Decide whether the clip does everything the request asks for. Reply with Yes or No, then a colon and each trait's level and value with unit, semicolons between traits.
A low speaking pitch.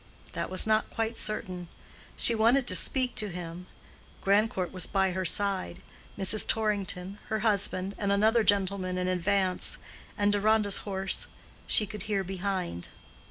No: high, 200 Hz